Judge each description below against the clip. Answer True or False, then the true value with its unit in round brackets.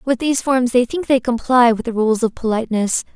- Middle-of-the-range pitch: False (240 Hz)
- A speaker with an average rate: False (230 wpm)